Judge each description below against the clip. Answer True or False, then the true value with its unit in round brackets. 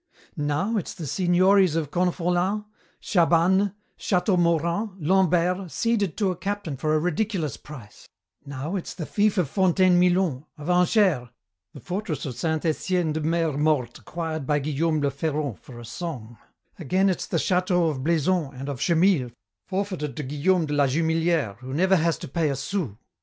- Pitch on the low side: False (165 Hz)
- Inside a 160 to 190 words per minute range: True (165 wpm)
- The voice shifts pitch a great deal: False (3.9 semitones)